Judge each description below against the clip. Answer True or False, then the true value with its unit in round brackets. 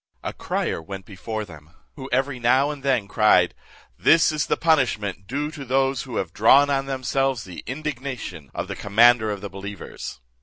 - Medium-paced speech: True (180 wpm)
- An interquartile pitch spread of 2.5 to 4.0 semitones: False (5.4 semitones)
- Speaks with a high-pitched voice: False (125 Hz)